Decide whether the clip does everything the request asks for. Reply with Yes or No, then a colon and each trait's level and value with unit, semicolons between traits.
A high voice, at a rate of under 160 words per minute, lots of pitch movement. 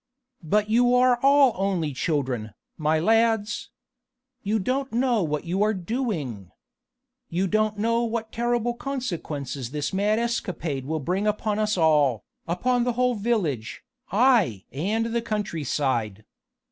Yes: high, 205 Hz; slow, 135 wpm; wide, 7.4 semitones